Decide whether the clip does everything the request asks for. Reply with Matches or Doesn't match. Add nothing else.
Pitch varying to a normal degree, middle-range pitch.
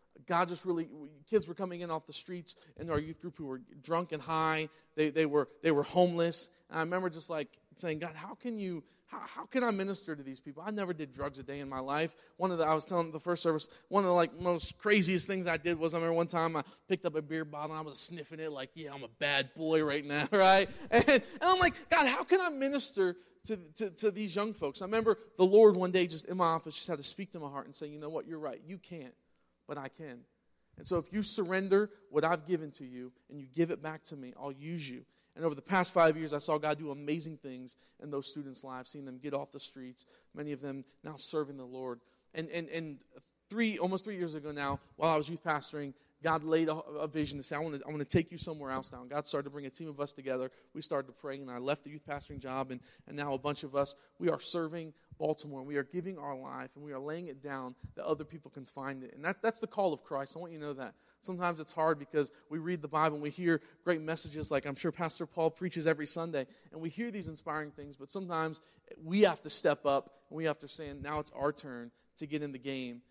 Matches